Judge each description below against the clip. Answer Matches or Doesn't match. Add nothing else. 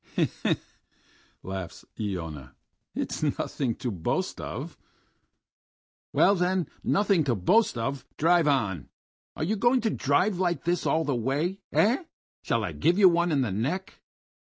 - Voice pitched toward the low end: Doesn't match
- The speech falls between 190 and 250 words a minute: Doesn't match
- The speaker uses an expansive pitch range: Matches